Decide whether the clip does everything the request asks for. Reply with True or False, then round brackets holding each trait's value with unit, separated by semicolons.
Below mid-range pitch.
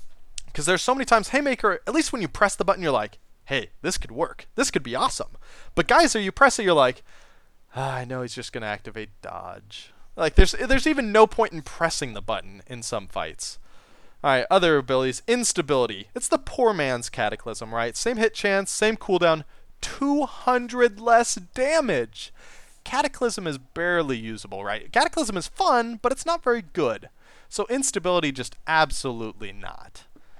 False (185 Hz)